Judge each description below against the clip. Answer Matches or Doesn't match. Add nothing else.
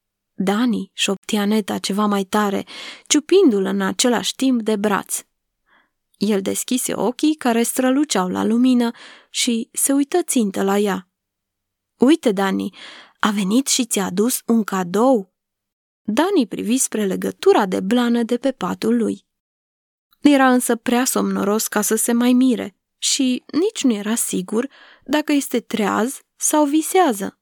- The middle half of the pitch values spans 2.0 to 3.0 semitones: Doesn't match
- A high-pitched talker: Matches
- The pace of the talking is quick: Doesn't match